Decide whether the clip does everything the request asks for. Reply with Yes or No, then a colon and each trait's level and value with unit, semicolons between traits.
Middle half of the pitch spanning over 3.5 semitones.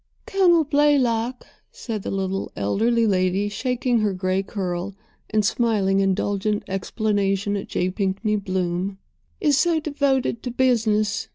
Yes: average, 4.2 semitones